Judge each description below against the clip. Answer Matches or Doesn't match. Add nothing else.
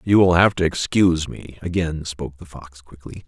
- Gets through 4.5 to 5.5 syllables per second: Matches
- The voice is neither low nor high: Doesn't match